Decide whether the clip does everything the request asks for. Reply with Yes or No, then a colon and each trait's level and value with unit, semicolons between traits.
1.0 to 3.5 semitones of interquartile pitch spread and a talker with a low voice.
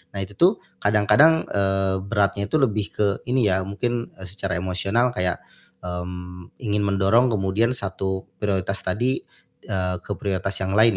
Yes: average, 3.0 semitones; low, 100 Hz